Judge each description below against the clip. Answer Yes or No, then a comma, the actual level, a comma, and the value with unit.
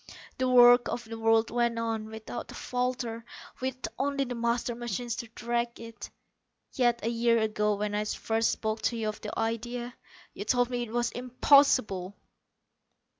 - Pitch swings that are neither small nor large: No, narrow, 1.6 semitones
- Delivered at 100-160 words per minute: No, average, 170 wpm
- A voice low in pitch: No, high, 235 Hz